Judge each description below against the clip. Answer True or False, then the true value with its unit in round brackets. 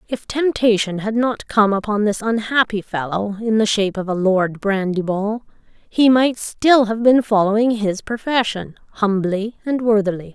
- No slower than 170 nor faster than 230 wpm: False (155 wpm)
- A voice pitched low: False (215 Hz)